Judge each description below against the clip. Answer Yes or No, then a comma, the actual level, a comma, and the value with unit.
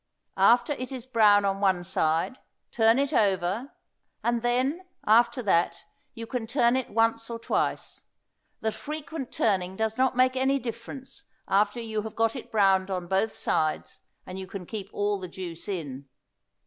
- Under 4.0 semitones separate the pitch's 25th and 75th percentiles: No, average, 4.4 semitones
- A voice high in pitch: Yes, high, 220 Hz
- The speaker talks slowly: No, average, 165 wpm